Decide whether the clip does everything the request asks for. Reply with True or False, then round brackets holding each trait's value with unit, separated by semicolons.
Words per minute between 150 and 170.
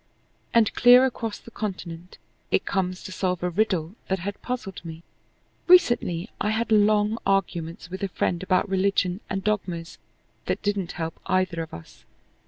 True (160 wpm)